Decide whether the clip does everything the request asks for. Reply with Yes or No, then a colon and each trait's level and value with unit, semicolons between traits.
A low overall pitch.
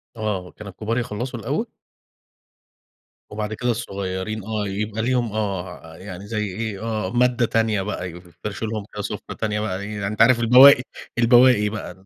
Yes: low, 105 Hz